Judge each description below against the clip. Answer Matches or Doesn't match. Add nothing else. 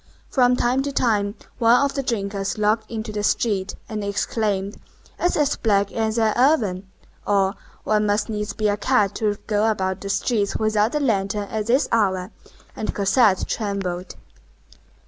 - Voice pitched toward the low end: Doesn't match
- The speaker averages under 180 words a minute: Matches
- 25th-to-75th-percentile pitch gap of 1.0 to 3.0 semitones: Matches